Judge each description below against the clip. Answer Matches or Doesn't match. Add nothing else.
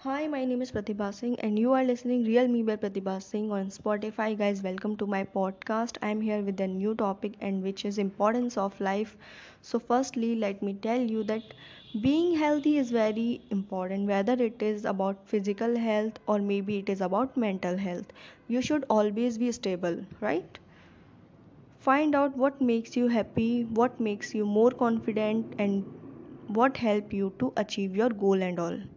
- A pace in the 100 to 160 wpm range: Doesn't match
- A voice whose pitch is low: Doesn't match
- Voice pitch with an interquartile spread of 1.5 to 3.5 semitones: Matches